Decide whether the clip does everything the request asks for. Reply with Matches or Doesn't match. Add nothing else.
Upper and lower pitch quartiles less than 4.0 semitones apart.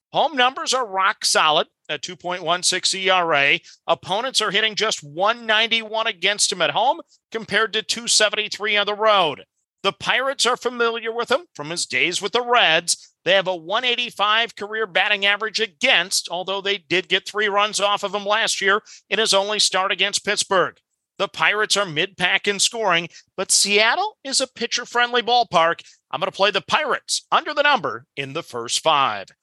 Matches